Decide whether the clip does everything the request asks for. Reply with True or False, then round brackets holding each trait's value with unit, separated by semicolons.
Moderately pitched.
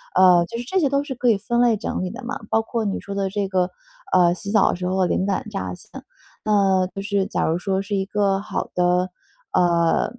False (195 Hz)